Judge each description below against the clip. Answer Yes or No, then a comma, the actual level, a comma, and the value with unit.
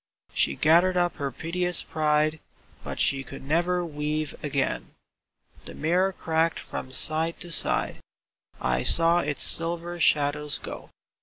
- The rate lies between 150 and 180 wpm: No, slow, 135 wpm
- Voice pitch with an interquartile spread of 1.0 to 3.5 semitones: Yes, average, 2.7 semitones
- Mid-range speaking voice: Yes, medium, 160 Hz